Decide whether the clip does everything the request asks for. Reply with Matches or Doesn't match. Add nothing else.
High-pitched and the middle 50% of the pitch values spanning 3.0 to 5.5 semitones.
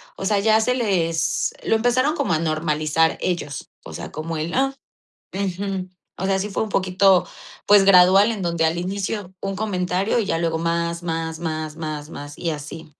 Doesn't match